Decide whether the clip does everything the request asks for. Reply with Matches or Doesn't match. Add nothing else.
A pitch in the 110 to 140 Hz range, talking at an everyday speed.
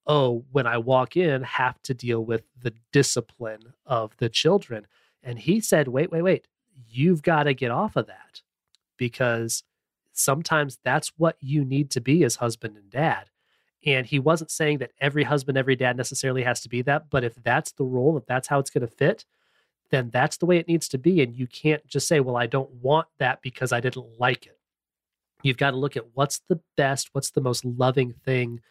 Doesn't match